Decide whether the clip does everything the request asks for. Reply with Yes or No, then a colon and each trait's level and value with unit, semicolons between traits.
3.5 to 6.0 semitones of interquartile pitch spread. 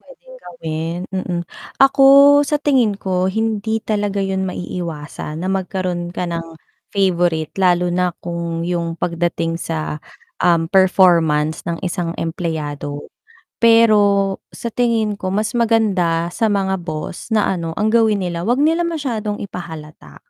Yes: average, 4.1 semitones